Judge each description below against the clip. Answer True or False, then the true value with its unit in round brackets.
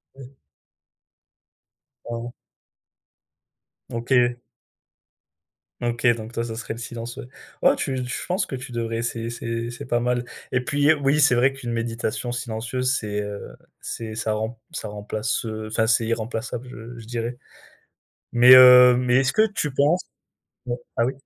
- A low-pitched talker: True (120 Hz)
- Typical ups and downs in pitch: False (1.9 semitones)